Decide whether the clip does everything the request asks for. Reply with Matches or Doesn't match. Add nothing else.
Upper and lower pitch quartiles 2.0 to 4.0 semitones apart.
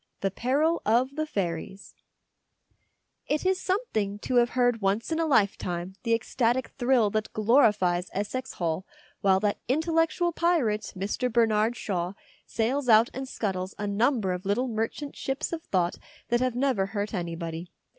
Doesn't match